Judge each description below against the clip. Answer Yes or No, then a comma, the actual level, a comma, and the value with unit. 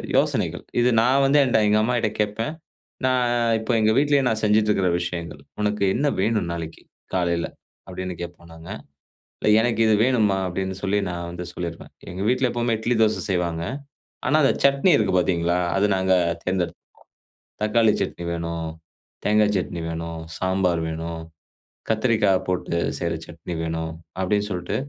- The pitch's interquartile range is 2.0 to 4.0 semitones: No, average, 4.5 semitones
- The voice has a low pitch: Yes, very low, 95 Hz